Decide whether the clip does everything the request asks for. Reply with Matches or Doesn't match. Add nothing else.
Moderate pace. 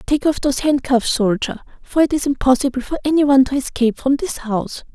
Matches